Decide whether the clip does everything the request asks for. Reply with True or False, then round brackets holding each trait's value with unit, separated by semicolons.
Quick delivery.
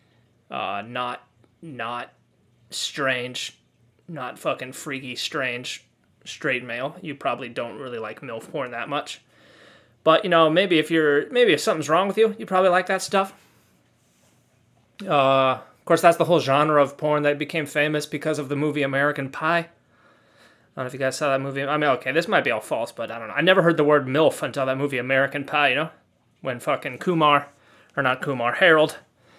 False (195 wpm)